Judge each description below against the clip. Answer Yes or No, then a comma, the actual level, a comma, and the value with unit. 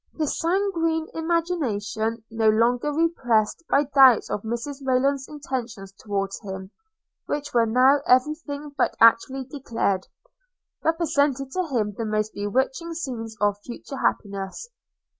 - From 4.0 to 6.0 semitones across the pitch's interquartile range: Yes, average, 5.2 semitones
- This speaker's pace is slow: Yes, slow, 125 wpm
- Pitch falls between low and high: No, very high, 255 Hz